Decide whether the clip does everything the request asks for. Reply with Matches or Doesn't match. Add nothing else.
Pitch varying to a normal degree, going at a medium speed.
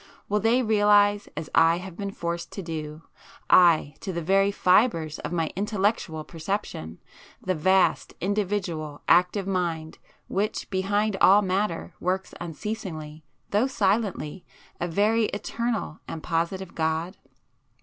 Doesn't match